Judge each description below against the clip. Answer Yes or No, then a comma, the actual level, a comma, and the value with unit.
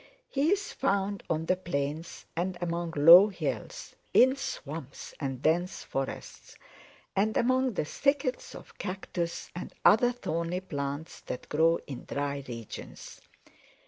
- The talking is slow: Yes, slow, 130 wpm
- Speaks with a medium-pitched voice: Yes, medium, 175 Hz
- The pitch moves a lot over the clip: Yes, wide, 5.7 semitones